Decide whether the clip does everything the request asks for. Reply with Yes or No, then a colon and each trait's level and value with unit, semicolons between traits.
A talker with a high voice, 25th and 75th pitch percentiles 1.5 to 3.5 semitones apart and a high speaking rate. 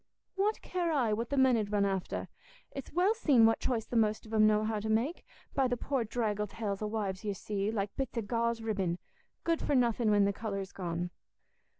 Yes: high, 220 Hz; average, 3.2 semitones; fast, 220 wpm